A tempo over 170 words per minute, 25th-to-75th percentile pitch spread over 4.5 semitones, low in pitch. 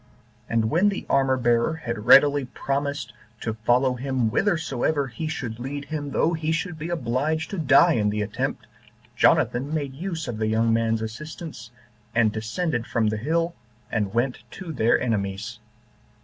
No: average, 165 wpm; wide, 5.6 semitones; low, 130 Hz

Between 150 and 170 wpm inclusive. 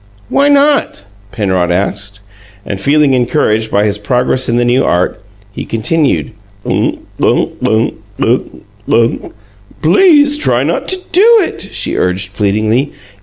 No: average, 140 wpm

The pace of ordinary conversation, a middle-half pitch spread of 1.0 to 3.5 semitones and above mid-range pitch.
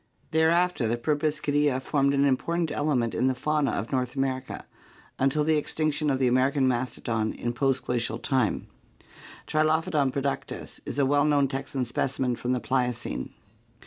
No: average, 150 wpm; average, 2.9 semitones; low, 135 Hz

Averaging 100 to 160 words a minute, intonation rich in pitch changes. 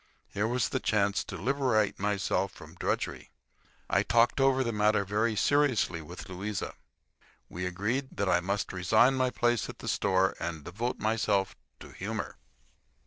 No: average, 155 wpm; average, 4.0 semitones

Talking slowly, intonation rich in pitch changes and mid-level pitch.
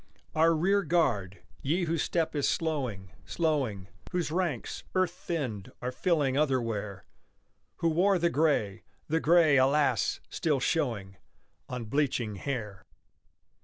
Yes: slow, 125 wpm; wide, 6.4 semitones; medium, 145 Hz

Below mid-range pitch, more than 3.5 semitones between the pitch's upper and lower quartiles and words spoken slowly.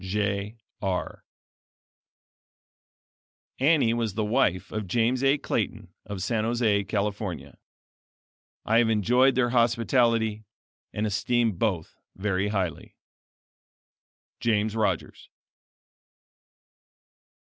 No: low, 110 Hz; average, 2.7 semitones; slow, 90 wpm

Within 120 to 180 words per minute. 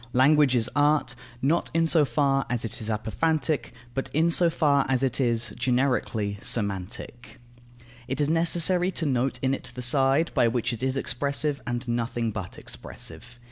Yes: average, 170 wpm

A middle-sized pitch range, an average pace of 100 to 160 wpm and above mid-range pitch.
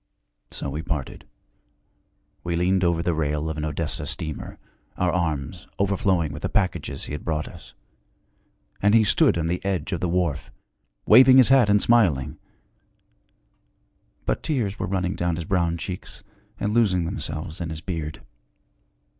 No: average, 3.9 semitones; average, 155 wpm; very low, 85 Hz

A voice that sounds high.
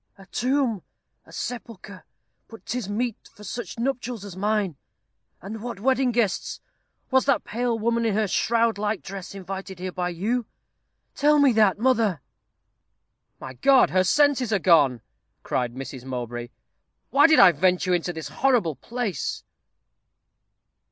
Yes: high, 210 Hz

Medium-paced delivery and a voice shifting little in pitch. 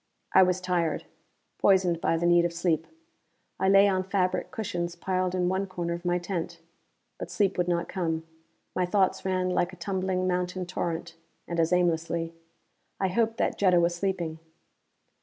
Yes: average, 170 wpm; narrow, 1.6 semitones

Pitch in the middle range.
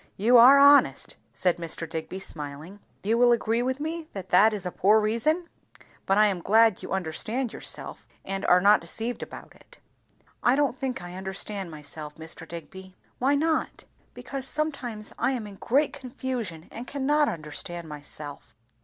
No: high, 210 Hz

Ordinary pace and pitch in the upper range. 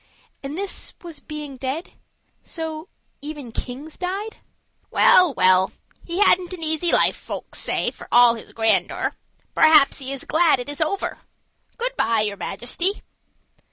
Yes: average, 145 wpm; very high, 305 Hz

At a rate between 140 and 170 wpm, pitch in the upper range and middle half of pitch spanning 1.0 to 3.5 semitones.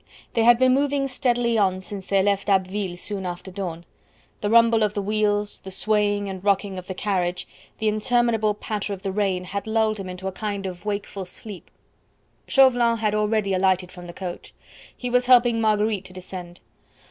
No: average, 185 wpm; high, 205 Hz; average, 2.8 semitones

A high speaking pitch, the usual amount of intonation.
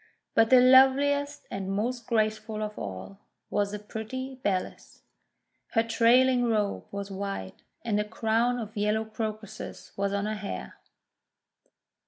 Yes: high, 220 Hz; average, 3.1 semitones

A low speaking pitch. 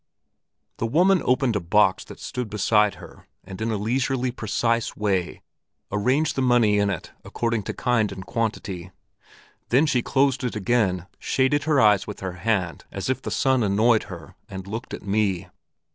Yes: low, 110 Hz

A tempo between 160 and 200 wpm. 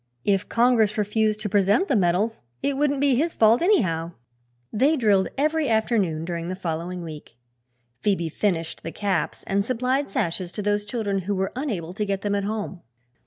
Yes: average, 175 wpm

